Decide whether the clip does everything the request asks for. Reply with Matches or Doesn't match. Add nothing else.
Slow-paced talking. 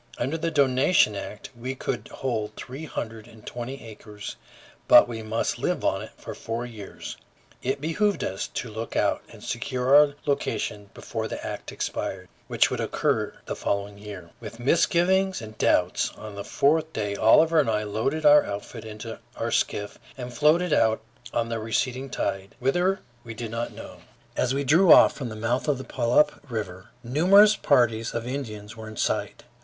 Doesn't match